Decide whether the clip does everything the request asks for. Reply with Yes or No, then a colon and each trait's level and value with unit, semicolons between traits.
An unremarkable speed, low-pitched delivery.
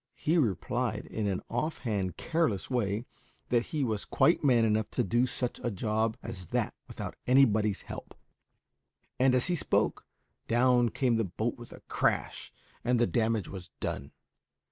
Yes: average, 160 wpm; low, 115 Hz